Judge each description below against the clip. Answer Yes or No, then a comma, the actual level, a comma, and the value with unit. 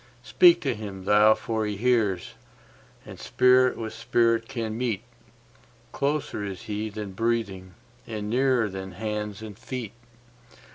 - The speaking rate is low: Yes, slow, 130 wpm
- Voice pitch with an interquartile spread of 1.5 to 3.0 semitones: Yes, narrow, 2.6 semitones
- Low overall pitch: Yes, low, 110 Hz